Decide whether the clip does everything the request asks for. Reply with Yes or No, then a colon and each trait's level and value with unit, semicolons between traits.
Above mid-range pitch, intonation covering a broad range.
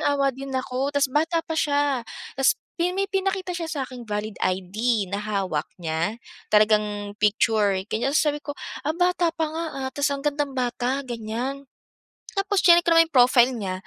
Yes: very high, 265 Hz; wide, 6.0 semitones